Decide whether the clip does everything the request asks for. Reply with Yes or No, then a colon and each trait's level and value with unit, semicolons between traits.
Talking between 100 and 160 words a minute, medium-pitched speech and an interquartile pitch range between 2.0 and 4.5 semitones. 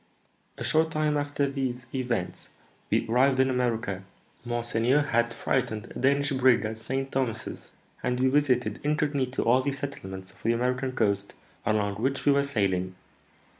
No: average, 155 wpm; low, 125 Hz; average, 3.5 semitones